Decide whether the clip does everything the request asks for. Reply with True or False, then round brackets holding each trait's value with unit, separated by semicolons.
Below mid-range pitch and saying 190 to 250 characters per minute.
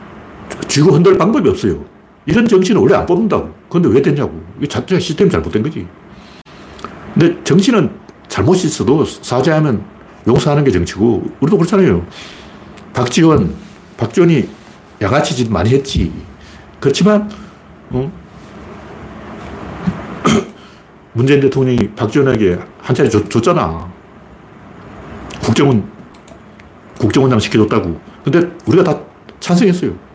False (130 Hz; 270 characters per minute)